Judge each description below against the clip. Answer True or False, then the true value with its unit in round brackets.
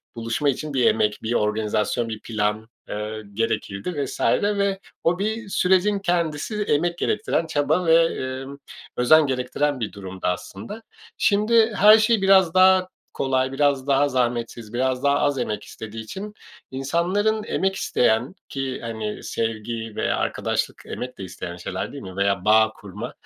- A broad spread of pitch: True (8.5 semitones)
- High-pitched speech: False (135 Hz)